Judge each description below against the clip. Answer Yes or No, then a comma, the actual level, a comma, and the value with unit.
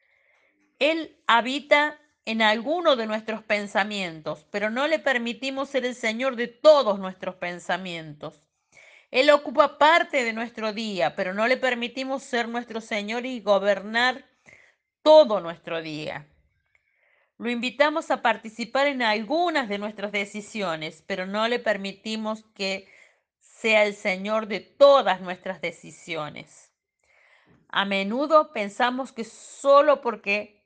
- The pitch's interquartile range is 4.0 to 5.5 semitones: Yes, average, 5.2 semitones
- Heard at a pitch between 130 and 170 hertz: No, high, 225 Hz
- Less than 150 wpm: Yes, slow, 125 wpm